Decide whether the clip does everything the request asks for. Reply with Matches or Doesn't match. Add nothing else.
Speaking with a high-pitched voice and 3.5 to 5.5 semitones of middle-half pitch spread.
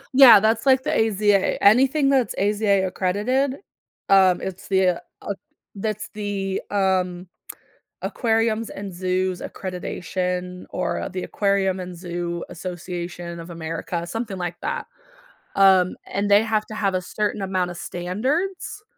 Doesn't match